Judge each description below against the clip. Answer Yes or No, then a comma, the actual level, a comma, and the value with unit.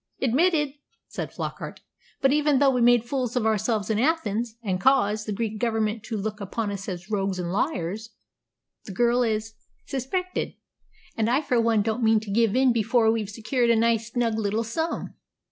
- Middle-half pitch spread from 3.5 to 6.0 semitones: No, average, 2.7 semitones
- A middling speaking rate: Yes, average, 180 wpm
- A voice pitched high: Yes, high, 225 Hz